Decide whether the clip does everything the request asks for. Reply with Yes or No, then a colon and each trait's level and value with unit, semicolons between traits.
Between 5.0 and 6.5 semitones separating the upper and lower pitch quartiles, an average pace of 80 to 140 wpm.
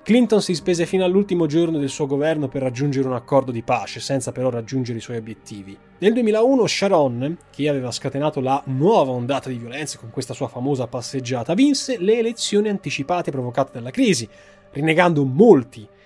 No: wide, 5.6 semitones; fast, 170 wpm